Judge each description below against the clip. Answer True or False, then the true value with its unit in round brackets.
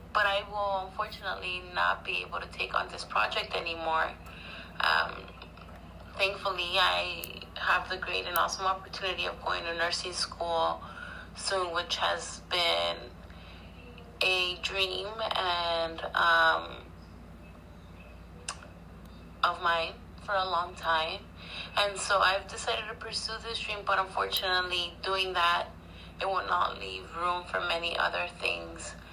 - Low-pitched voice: False (165 Hz)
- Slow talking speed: True (130 wpm)